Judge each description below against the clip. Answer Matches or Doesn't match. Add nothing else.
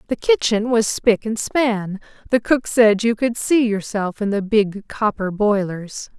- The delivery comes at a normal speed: Matches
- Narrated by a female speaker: Matches